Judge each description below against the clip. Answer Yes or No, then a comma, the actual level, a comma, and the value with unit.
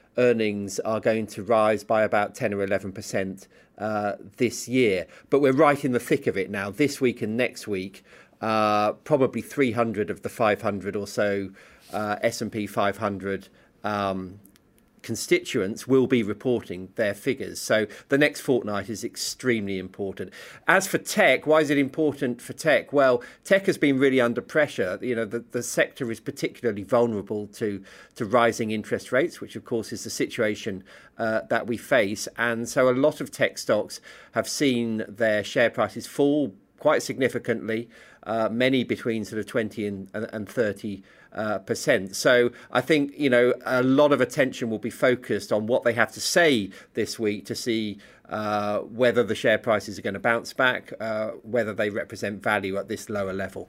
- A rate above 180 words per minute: No, average, 175 wpm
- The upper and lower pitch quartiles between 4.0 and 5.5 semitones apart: No, average, 3.3 semitones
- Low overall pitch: Yes, low, 115 Hz